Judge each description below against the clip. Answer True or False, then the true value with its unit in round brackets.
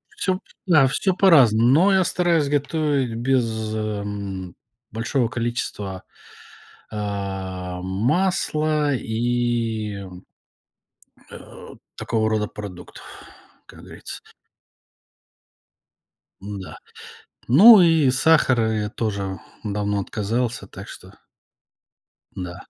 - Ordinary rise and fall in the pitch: False (5.9 semitones)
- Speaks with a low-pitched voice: True (115 Hz)